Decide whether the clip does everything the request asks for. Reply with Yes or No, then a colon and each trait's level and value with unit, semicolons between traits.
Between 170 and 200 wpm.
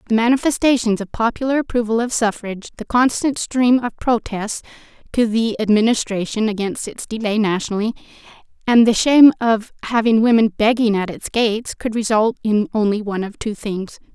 No: average, 155 wpm